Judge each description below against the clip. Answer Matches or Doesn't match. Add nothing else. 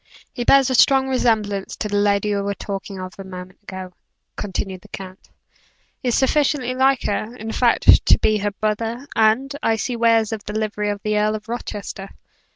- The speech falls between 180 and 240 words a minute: Matches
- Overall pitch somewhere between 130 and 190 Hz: Doesn't match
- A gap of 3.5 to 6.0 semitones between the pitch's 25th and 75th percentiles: Doesn't match